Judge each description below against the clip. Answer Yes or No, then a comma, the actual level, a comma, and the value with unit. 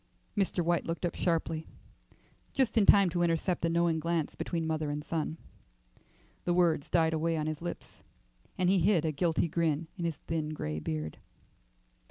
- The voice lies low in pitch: No, medium, 165 Hz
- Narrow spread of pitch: Yes, narrow, 1.8 semitones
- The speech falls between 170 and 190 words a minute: Yes, average, 175 wpm